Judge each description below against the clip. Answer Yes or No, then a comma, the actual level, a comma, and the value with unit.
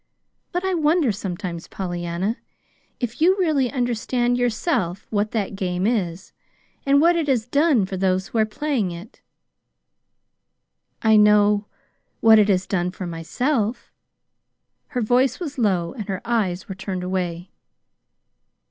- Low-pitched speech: No, high, 215 Hz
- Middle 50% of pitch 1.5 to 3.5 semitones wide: No, average, 5.2 semitones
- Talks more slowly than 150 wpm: Yes, average, 140 wpm